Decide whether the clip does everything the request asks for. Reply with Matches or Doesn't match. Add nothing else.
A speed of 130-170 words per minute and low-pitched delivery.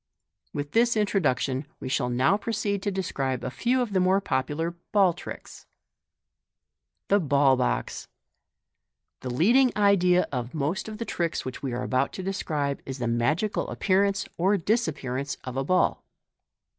Doesn't match